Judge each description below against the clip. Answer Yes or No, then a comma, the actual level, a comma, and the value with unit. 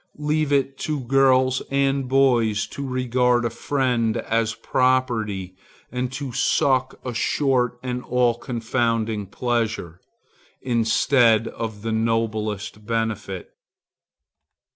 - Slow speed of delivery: Yes, slow, 105 wpm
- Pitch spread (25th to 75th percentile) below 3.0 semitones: Yes, narrow, 2.6 semitones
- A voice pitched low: Yes, low, 120 Hz